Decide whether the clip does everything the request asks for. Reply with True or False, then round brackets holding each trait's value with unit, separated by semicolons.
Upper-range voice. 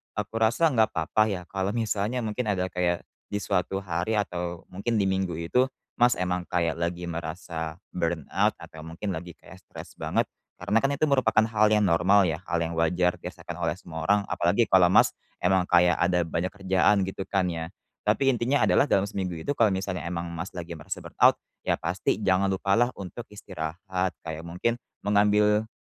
False (95 Hz)